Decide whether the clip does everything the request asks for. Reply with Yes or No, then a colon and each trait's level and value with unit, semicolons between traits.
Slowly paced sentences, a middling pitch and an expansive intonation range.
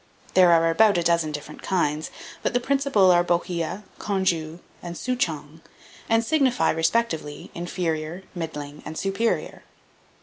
No: slow, 130 wpm; medium, 175 Hz; average, 4.3 semitones